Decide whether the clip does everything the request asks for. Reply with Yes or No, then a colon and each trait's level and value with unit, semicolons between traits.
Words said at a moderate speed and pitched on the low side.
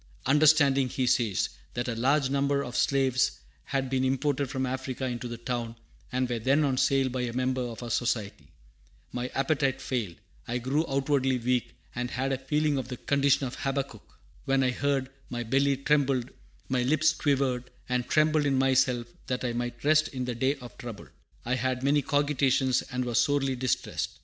Yes: average, 185 wpm; low, 130 Hz